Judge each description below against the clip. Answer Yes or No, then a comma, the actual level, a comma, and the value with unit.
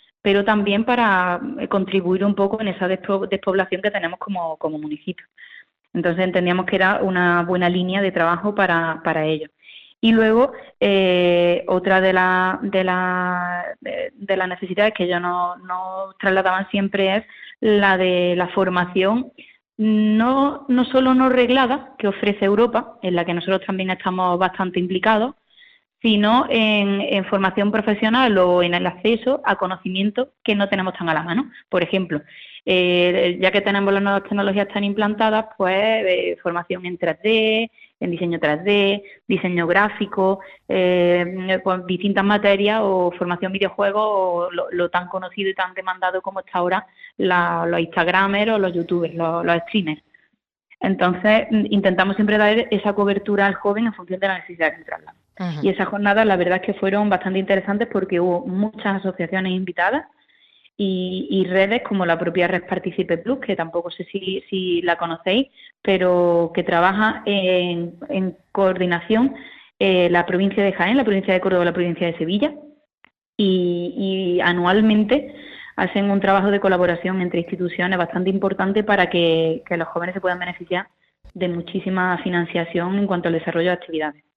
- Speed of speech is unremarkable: Yes, average, 160 wpm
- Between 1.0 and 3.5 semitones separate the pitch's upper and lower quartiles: Yes, narrow, 2.5 semitones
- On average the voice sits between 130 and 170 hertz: No, high, 190 Hz